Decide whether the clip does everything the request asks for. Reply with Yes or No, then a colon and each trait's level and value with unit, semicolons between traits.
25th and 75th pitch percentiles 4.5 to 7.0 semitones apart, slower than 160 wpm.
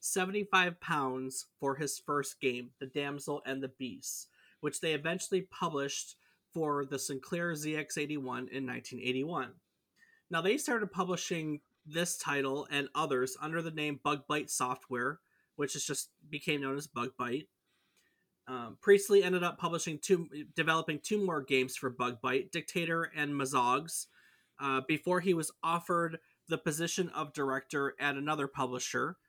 No: average, 3.8 semitones; average, 140 wpm